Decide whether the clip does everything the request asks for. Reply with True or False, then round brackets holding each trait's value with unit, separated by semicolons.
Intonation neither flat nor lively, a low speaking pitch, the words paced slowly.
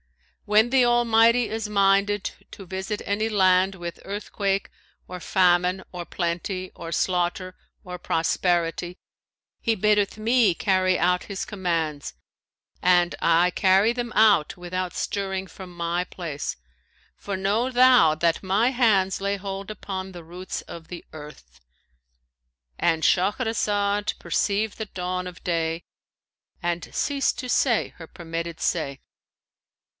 False (3.0 semitones; 190 Hz; 130 wpm)